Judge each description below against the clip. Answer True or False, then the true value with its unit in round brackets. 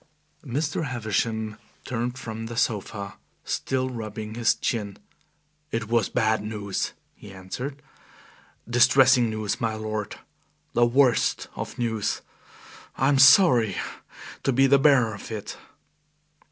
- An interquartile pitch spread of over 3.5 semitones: False (3.0 semitones)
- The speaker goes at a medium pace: False (120 wpm)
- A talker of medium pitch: False (115 Hz)